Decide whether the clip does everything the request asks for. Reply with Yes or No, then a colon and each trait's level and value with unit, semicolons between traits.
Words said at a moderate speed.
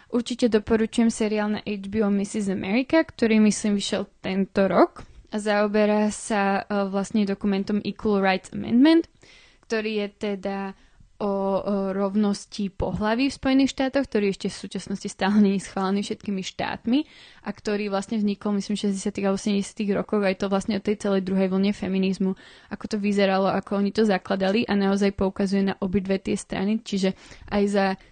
Yes: average, 155 wpm